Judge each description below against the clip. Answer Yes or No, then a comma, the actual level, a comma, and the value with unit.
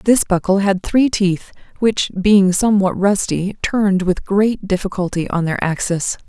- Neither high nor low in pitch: No, high, 195 Hz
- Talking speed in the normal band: Yes, average, 155 wpm